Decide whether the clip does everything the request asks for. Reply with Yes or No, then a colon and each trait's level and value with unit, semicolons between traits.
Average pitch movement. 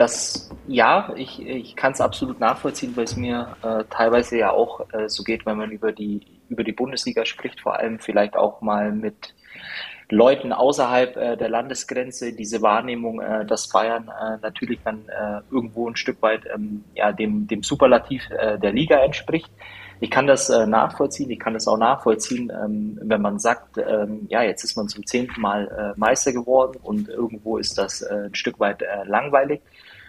No: narrow, 2.3 semitones